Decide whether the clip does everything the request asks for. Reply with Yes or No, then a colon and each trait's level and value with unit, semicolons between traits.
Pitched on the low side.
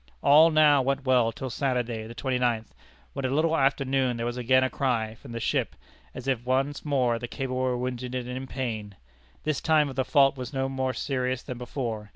Yes: low, 130 Hz